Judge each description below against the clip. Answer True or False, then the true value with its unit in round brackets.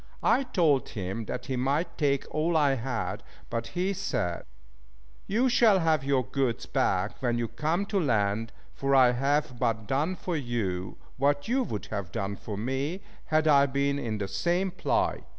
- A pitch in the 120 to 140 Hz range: True (135 Hz)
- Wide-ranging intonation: True (6.0 semitones)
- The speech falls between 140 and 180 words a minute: True (175 wpm)